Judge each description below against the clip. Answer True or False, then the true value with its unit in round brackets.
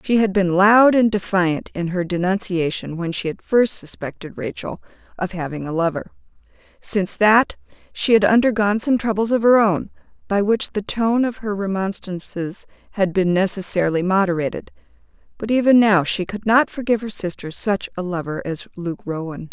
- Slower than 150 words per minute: False (170 wpm)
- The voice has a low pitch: False (195 Hz)